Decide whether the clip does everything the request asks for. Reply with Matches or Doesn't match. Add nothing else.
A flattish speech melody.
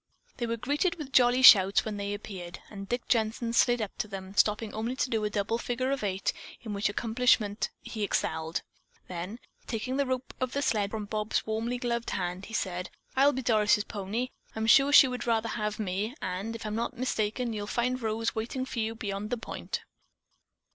Doesn't match